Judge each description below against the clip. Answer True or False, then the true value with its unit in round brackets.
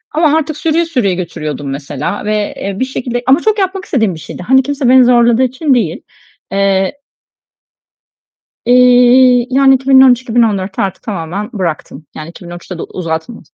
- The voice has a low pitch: False (240 Hz)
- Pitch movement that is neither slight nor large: False (6.0 semitones)